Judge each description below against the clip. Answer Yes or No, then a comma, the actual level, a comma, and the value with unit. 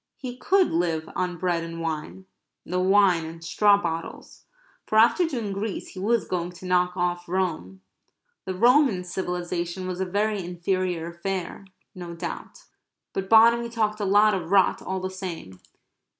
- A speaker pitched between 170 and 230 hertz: Yes, medium, 185 Hz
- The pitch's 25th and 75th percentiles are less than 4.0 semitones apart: Yes, average, 3.0 semitones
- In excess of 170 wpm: No, average, 160 wpm